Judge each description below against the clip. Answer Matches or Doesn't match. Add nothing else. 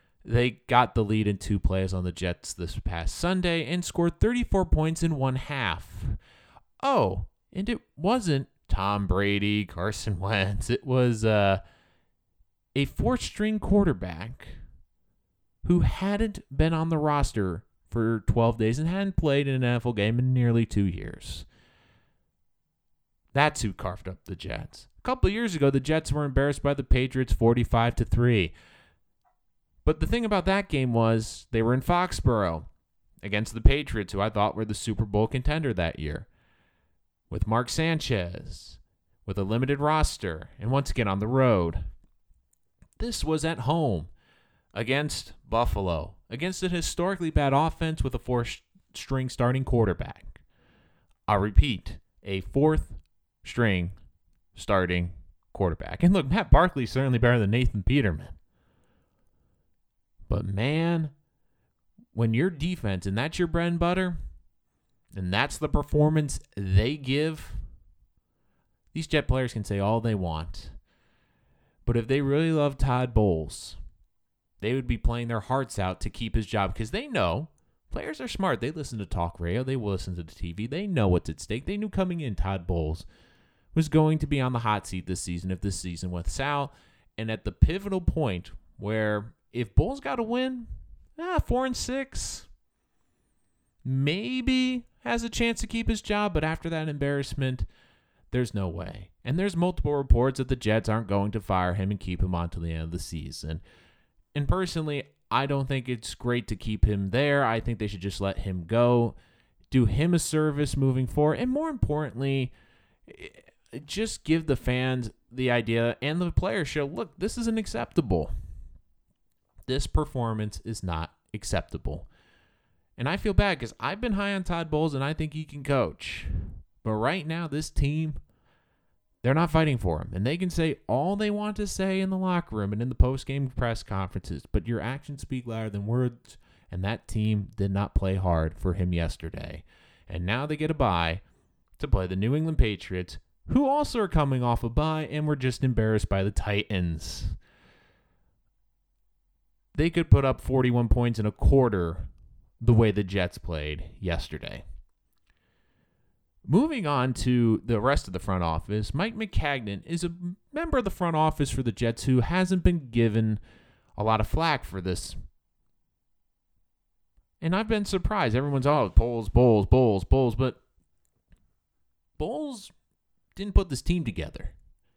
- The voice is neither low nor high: Doesn't match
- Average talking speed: Matches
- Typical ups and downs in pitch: Doesn't match